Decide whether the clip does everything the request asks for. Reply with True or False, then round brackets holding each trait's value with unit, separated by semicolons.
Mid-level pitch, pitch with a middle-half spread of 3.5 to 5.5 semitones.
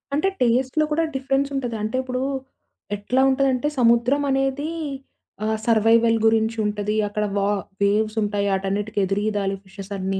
False (225 Hz; 4.1 semitones)